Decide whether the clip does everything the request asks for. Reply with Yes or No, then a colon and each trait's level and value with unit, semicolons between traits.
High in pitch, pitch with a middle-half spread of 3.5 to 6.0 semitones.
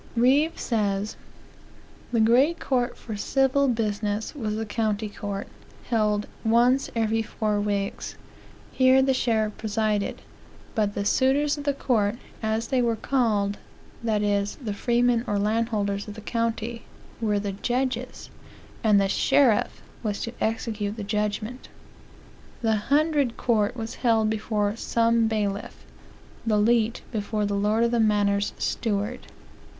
No: high, 220 Hz; narrow, 2.5 semitones